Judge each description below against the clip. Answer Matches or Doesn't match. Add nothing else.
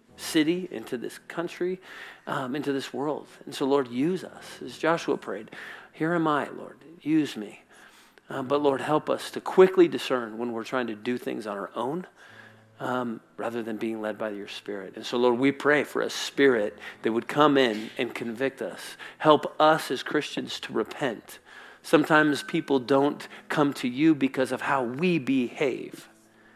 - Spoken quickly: Doesn't match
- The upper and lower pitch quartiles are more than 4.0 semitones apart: Matches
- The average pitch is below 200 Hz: Matches